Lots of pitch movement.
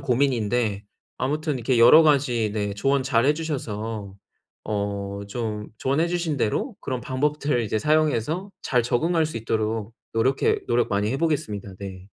Yes: wide, 5.7 semitones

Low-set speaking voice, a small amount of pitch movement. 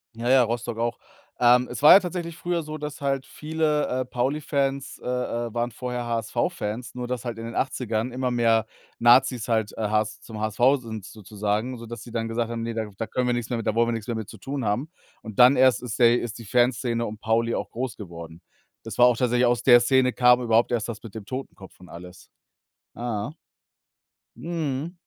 Yes: low, 120 Hz; narrow, 2.2 semitones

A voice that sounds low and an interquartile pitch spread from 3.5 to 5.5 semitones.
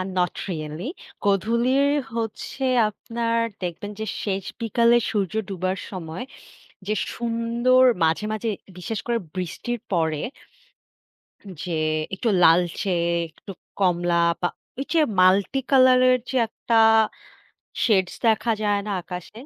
No: high, 205 Hz; average, 4.5 semitones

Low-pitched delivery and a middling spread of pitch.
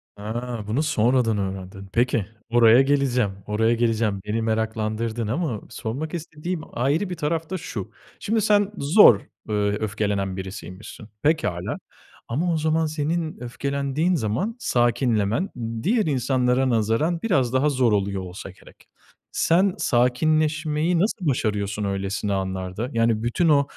No: low, 120 Hz; wide, 6.5 semitones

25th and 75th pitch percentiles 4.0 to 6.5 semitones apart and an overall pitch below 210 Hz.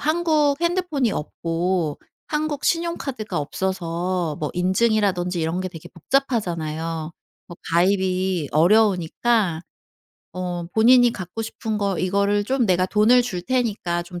Yes: wide, 5.6 semitones; high, 190 Hz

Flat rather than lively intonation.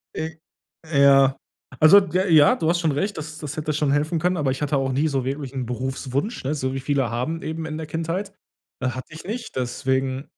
No: average, 3.2 semitones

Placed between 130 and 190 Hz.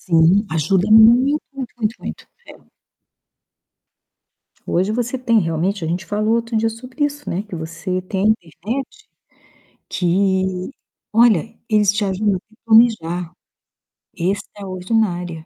No: high, 205 Hz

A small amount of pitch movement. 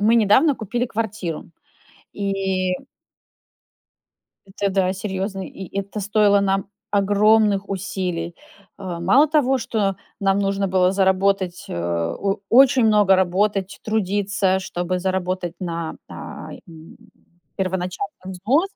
Yes: narrow, 2.0 semitones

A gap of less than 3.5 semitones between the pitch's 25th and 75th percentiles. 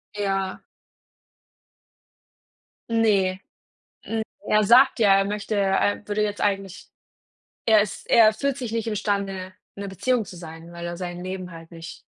Yes: narrow, 2.4 semitones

